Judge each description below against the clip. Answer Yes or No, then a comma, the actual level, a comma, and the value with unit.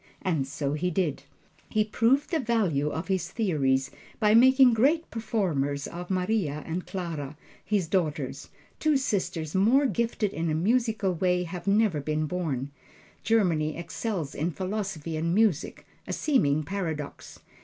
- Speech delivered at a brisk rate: No, average, 145 wpm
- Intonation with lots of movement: Yes, wide, 6.0 semitones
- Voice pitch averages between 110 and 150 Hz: No, medium, 180 Hz